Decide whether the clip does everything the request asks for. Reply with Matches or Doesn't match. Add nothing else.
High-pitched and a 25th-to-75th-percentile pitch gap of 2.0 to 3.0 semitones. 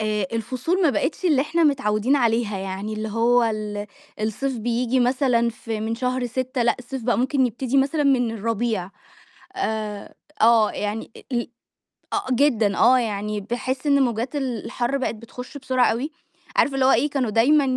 Doesn't match